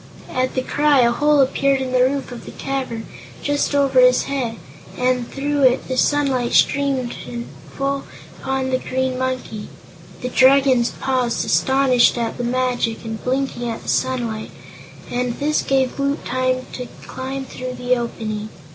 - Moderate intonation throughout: No, narrow, 1.8 semitones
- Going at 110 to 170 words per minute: Yes, average, 155 wpm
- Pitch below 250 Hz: No, very high, 255 Hz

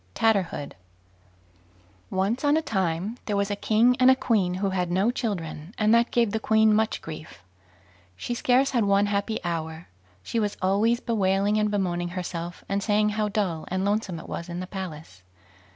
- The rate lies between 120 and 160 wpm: No, average, 180 wpm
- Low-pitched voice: No, high, 200 Hz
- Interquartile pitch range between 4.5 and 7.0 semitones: No, average, 3.6 semitones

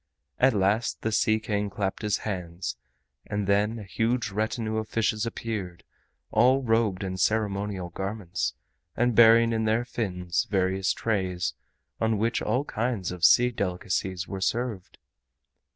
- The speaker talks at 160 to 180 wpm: No, average, 140 wpm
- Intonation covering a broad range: No, average, 3.1 semitones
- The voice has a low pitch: Yes, low, 105 Hz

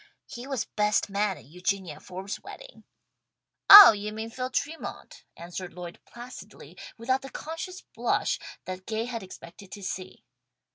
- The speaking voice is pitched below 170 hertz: No, high, 210 Hz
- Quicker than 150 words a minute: No, average, 145 wpm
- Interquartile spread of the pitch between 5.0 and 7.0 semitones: Yes, wide, 5.4 semitones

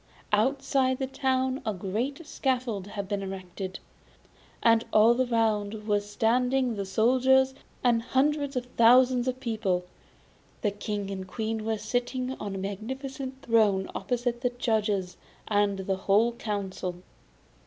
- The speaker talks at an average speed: No, slow, 130 wpm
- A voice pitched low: No, high, 225 Hz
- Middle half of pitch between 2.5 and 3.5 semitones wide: No, average, 4.1 semitones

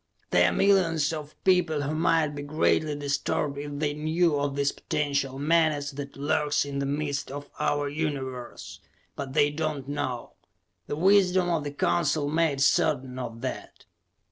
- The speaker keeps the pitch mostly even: Yes, narrow, 1.9 semitones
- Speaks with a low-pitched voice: No, medium, 145 Hz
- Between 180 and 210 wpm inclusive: No, average, 165 wpm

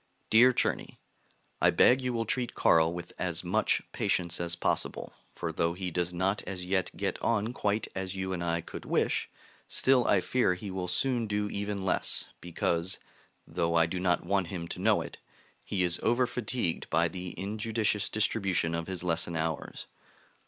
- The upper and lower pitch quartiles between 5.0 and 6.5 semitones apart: No, average, 3.6 semitones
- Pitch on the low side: Yes, very low, 95 Hz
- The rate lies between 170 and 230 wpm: Yes, average, 180 wpm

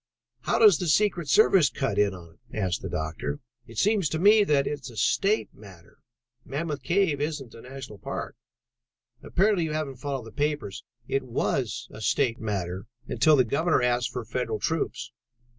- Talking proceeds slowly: No, average, 175 wpm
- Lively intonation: Yes, wide, 6.2 semitones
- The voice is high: No, low, 135 Hz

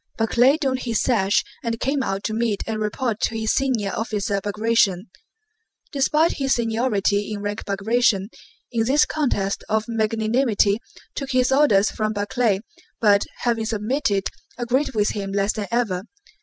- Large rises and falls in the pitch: No, average, 3.3 semitones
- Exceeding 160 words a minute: No, average, 150 wpm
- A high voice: Yes, high, 220 Hz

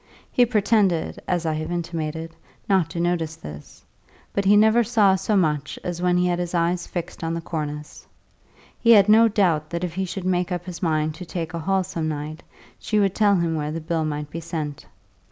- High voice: No, medium, 170 Hz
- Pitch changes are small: No, average, 3.2 semitones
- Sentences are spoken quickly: Yes, fast, 210 wpm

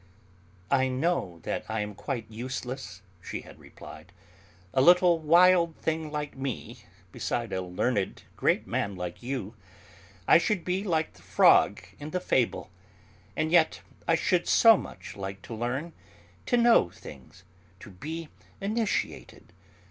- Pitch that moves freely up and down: Yes, wide, 7.9 semitones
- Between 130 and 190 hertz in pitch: Yes, low, 135 Hz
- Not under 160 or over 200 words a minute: No, average, 140 wpm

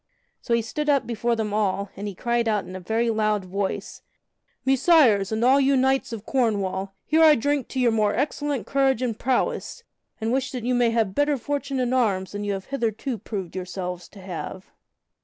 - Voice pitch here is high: Yes, high, 230 Hz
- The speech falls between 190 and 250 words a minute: Yes, average, 195 wpm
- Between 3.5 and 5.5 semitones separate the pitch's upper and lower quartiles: Yes, average, 4.8 semitones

